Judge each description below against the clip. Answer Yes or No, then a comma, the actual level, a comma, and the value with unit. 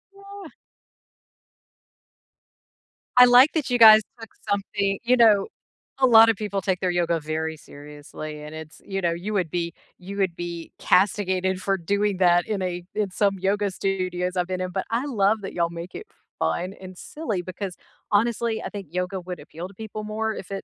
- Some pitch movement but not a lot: Yes, average, 3.2 semitones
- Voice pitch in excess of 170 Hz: Yes, high, 190 Hz